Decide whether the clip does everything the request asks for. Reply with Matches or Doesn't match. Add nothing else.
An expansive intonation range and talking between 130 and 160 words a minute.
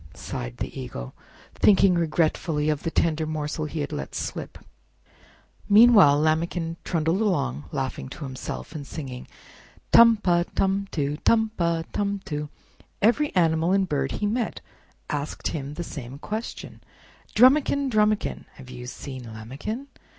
Matches